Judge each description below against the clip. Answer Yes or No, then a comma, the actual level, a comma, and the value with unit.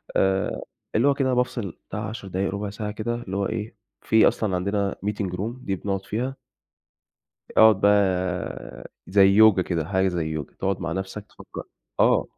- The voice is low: Yes, low, 100 Hz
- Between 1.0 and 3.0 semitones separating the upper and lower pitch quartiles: Yes, narrow, 2.5 semitones